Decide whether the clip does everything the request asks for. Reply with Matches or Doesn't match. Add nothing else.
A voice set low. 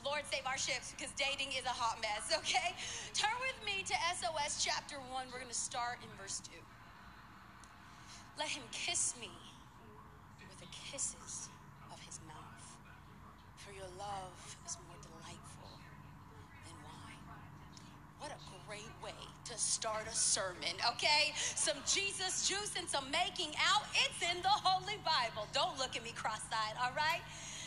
Doesn't match